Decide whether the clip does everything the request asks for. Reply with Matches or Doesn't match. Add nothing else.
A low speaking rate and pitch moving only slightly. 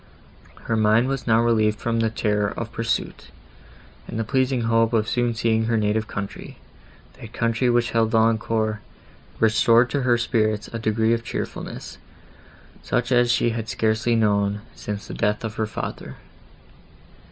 Doesn't match